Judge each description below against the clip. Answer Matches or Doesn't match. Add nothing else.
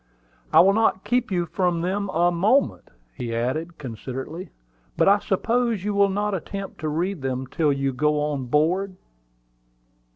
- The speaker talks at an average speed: Matches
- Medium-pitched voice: Matches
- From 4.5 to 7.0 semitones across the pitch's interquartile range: Matches